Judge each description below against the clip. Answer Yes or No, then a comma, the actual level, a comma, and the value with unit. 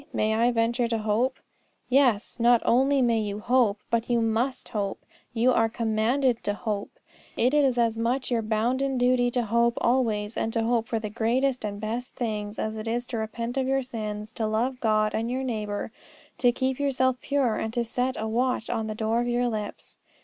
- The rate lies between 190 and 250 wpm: Yes, average, 200 wpm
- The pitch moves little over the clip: Yes, narrow, 2.3 semitones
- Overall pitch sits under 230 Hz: No, high, 235 Hz